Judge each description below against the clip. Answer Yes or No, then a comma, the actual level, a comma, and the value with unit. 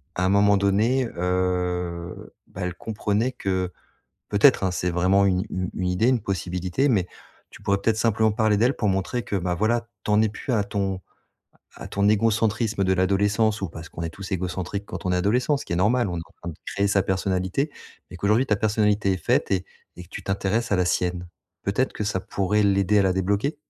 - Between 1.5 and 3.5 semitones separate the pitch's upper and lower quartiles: Yes, average, 2.9 semitones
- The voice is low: Yes, low, 100 Hz